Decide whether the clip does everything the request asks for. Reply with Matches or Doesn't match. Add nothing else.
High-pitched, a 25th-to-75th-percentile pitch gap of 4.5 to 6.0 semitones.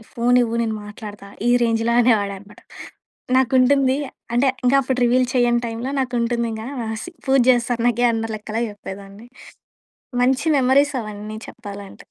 Doesn't match